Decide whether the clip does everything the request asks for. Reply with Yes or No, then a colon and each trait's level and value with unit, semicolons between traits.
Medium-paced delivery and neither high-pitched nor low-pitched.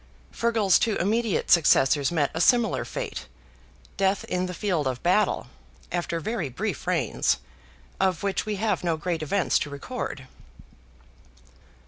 No: slow, 125 wpm; medium, 180 Hz